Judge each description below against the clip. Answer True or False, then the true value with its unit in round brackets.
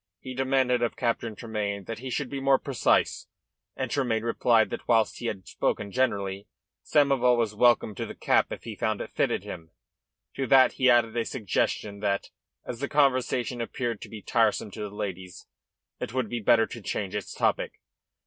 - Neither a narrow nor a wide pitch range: True (3.7 semitones)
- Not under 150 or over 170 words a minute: False (185 wpm)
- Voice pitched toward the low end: True (115 Hz)